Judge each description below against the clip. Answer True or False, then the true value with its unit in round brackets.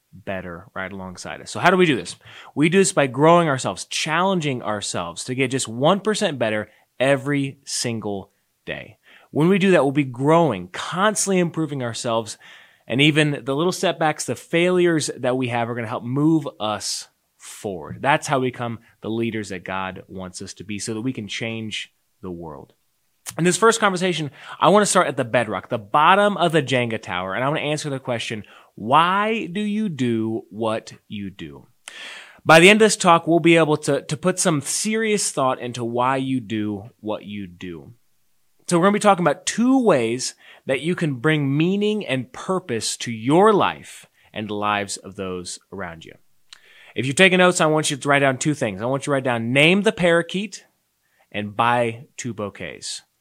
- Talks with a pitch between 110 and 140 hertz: True (135 Hz)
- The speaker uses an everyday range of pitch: False (7.2 semitones)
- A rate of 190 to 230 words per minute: True (200 wpm)